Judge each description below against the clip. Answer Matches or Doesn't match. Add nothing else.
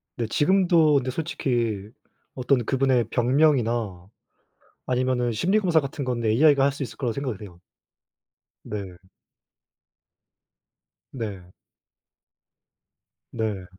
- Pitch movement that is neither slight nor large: Matches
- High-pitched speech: Doesn't match